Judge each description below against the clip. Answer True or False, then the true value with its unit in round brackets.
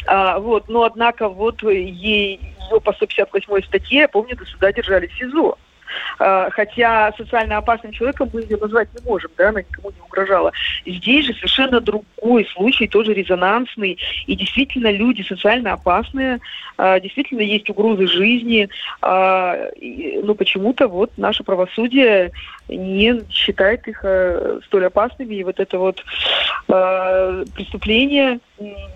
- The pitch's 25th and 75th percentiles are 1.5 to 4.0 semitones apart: True (3.6 semitones)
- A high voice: True (210 Hz)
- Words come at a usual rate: True (140 wpm)